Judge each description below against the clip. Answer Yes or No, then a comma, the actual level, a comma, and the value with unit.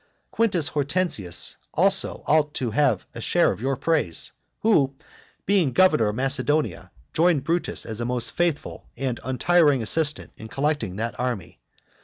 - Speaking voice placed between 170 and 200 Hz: No, medium, 140 Hz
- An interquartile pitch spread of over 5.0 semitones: Yes, wide, 5.5 semitones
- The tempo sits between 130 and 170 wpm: Yes, average, 145 wpm